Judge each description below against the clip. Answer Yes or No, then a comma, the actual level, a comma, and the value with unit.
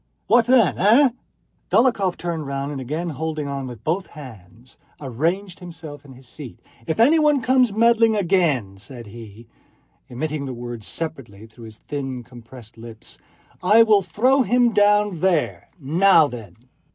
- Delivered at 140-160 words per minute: Yes, average, 150 wpm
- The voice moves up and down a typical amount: No, wide, 8.7 semitones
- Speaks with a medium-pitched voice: Yes, medium, 155 Hz